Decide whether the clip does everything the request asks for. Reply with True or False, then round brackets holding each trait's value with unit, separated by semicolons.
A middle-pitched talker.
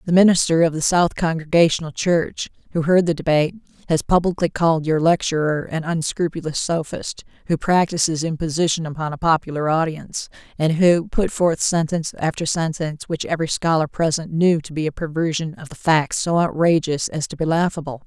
True (160 Hz)